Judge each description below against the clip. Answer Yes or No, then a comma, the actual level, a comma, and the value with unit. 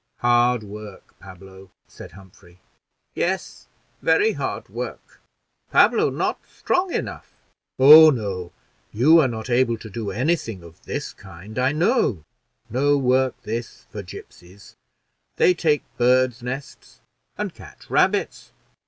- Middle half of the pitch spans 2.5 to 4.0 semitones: No, wide, 5.6 semitones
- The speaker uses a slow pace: Yes, slow, 125 wpm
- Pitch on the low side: Yes, low, 120 Hz